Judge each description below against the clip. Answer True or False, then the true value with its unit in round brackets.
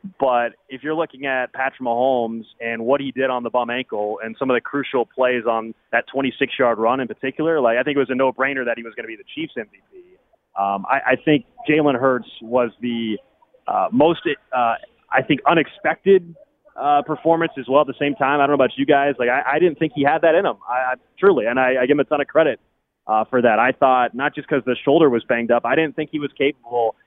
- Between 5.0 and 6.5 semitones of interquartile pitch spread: False (3.8 semitones)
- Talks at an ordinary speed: False (255 wpm)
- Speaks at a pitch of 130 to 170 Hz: True (135 Hz)